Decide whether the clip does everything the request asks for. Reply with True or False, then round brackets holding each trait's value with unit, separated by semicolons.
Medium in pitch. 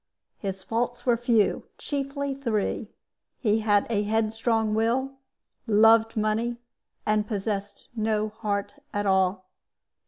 False (220 Hz)